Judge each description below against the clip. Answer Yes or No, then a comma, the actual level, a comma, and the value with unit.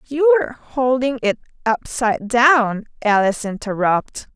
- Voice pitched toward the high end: Yes, high, 240 Hz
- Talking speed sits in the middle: No, slow, 95 wpm